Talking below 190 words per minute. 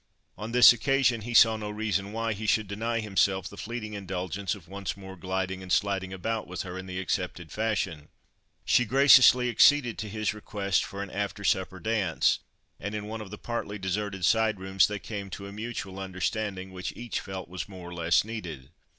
No: average, 195 wpm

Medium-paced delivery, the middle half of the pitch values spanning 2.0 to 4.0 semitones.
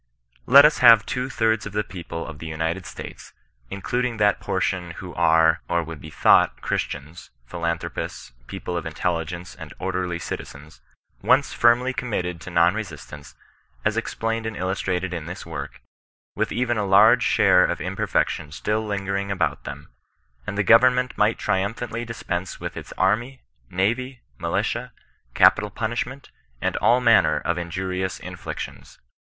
No: average, 150 wpm; average, 5.1 semitones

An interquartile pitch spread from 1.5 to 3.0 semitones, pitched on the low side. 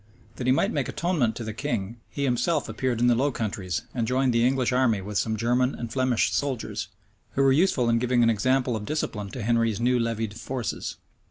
Yes: narrow, 2.5 semitones; low, 120 Hz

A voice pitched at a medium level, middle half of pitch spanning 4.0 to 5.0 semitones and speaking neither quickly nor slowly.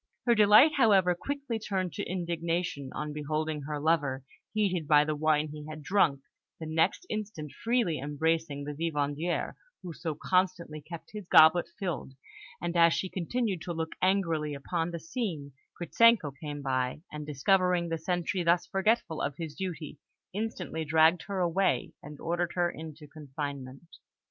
No: medium, 165 Hz; average, 3.6 semitones; average, 155 wpm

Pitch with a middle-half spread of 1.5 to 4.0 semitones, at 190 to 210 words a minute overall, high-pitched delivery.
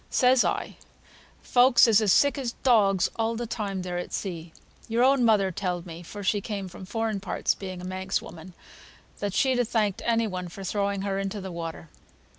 Yes: average, 3.6 semitones; average, 200 wpm; high, 200 Hz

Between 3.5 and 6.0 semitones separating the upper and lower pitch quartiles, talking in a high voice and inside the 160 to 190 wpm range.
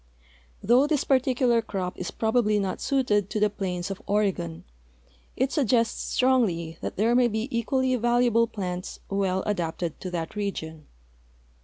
No: average, 4.9 semitones; high, 210 Hz; average, 145 wpm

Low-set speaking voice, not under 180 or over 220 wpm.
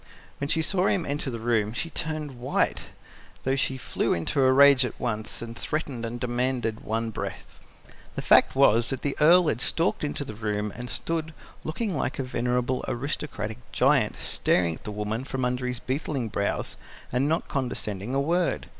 Yes: low, 130 Hz; average, 185 wpm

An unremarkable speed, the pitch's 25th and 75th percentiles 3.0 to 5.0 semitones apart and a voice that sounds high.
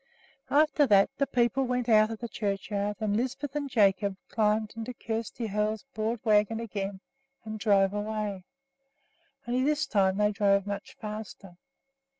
No: average, 150 wpm; narrow, 2.6 semitones; high, 215 Hz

